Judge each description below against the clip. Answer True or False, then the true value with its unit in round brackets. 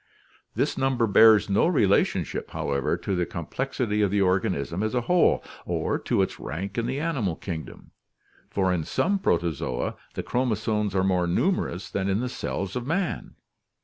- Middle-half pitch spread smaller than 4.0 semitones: False (5.4 semitones)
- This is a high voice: False (100 Hz)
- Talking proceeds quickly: False (165 wpm)